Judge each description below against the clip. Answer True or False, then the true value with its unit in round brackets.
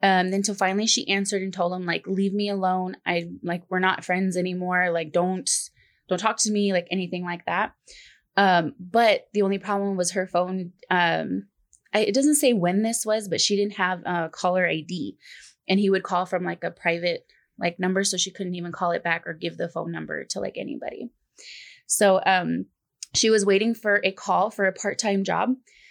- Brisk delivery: True (210 wpm)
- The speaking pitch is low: False (190 Hz)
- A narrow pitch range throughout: True (2.2 semitones)